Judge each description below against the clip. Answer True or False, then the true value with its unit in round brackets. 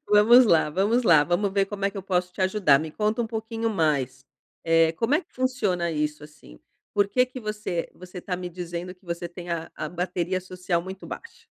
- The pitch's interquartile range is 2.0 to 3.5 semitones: False (3.9 semitones)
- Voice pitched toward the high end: False (180 Hz)